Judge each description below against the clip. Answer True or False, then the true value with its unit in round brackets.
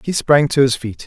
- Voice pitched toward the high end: False (135 Hz)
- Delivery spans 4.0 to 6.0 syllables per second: True (5.2 syllables/s)